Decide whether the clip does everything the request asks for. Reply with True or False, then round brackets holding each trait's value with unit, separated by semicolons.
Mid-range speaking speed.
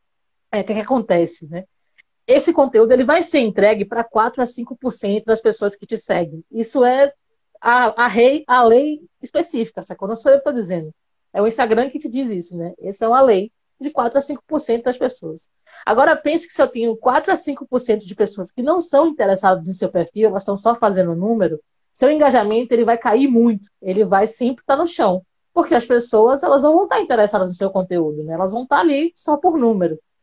False (225 wpm)